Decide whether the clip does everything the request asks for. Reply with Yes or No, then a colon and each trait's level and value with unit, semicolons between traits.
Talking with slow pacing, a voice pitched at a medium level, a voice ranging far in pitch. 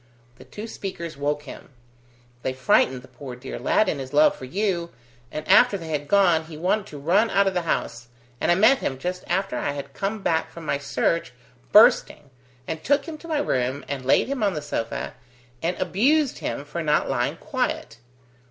No: average, 200 wpm; medium, 165 Hz; wide, 5.9 semitones